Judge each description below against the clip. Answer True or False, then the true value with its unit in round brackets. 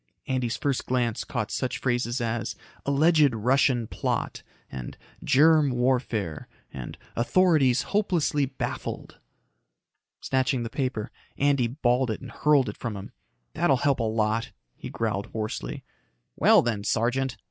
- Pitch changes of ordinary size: True (3.2 semitones)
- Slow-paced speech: True (130 wpm)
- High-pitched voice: False (125 Hz)